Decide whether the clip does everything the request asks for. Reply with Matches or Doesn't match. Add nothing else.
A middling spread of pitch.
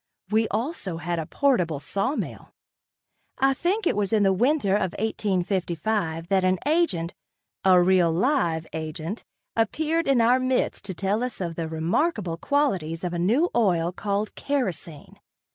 Doesn't match